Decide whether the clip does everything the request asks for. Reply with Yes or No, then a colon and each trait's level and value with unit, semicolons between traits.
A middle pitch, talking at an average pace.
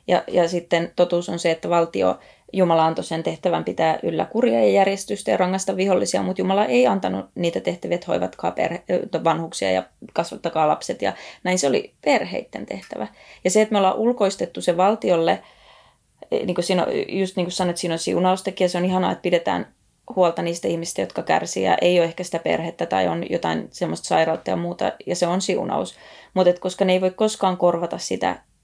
No: medium, 175 Hz; fast, 190 wpm